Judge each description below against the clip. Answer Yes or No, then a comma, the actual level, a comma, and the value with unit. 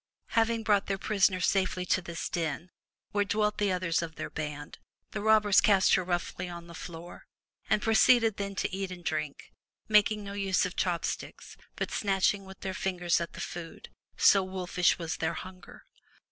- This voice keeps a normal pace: Yes, average, 180 wpm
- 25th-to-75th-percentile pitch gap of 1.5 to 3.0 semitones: Yes, average, 2.7 semitones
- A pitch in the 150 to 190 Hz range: Yes, medium, 185 Hz